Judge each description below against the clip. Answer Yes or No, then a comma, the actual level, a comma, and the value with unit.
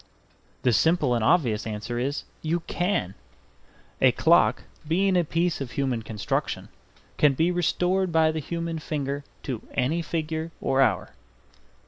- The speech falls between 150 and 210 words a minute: No, average, 140 wpm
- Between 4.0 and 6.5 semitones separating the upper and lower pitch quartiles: Yes, average, 4.8 semitones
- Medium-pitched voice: Yes, medium, 155 Hz